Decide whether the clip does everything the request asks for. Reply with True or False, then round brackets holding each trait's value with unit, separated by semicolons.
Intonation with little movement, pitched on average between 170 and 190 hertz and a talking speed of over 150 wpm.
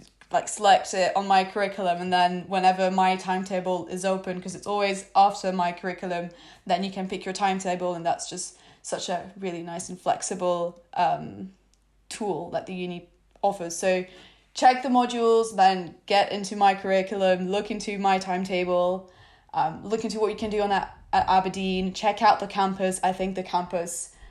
True (1.7 semitones; 185 Hz; 180 wpm)